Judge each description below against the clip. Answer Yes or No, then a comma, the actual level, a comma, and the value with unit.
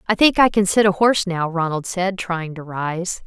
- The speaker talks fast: Yes, fast, 240 wpm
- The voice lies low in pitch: No, medium, 185 Hz